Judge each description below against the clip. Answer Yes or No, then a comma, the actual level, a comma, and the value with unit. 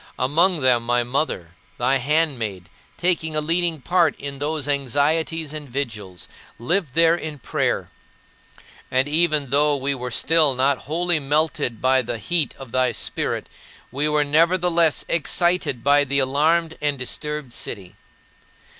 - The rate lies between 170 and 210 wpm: No, average, 140 wpm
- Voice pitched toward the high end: No, medium, 145 Hz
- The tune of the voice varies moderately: Yes, average, 3.8 semitones